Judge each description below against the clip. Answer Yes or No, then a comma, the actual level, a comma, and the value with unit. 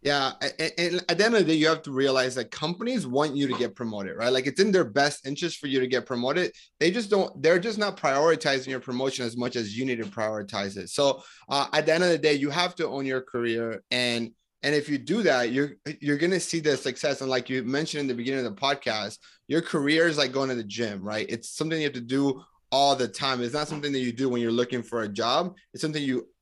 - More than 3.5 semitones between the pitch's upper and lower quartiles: Yes, average, 4.2 semitones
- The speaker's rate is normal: No, fast, 270 wpm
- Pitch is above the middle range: No, medium, 140 Hz